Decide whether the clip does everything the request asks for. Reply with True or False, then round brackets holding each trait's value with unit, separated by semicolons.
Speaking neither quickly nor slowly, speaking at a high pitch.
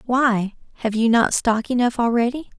True (160 wpm; 235 Hz)